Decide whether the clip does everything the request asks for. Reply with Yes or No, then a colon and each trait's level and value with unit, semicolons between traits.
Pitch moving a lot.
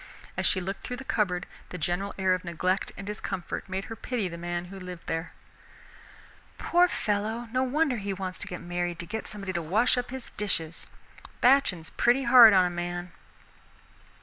No: average, 4.6 semitones